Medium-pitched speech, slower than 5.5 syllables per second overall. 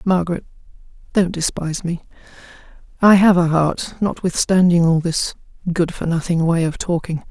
Yes: medium, 175 Hz; 5.1 syllables/s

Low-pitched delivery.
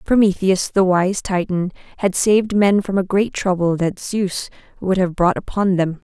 No: high, 190 Hz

